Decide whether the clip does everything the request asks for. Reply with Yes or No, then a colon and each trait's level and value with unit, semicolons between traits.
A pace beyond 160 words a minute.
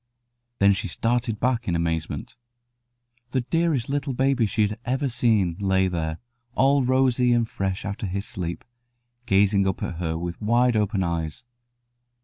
No: average, 150 wpm